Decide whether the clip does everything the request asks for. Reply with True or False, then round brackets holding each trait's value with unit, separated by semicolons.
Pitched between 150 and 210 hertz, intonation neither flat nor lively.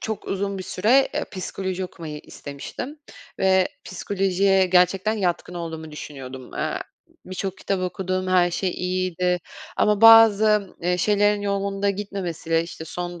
False (185 Hz; 2.2 semitones)